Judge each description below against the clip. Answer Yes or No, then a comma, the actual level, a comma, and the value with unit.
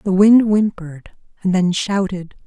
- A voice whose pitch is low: No, high, 190 Hz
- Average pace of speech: Yes, average, 145 wpm